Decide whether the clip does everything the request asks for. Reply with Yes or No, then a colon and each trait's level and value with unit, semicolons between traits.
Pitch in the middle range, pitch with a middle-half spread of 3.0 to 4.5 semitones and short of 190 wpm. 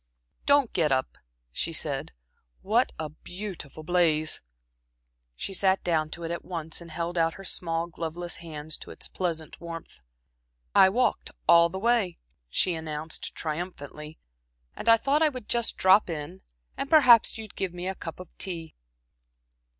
Yes: medium, 170 Hz; average, 3.3 semitones; average, 160 wpm